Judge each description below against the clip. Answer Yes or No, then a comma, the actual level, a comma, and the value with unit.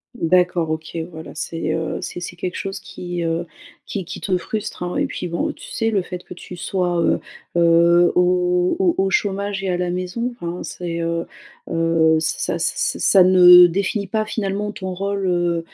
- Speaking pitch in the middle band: Yes, medium, 180 Hz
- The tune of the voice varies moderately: No, narrow, 2.3 semitones